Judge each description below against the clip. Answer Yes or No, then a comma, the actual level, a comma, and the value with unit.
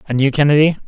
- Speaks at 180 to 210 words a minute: Yes, fast, 205 wpm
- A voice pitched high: No, medium, 145 Hz